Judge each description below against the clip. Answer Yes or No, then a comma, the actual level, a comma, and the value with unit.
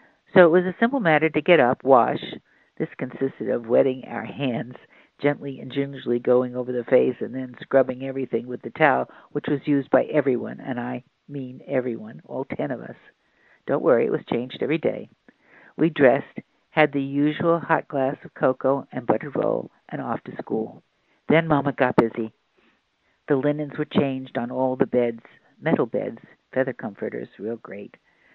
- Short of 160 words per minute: No, average, 180 wpm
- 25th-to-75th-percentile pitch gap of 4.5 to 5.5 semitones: No, average, 3.0 semitones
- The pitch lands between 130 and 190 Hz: Yes, low, 135 Hz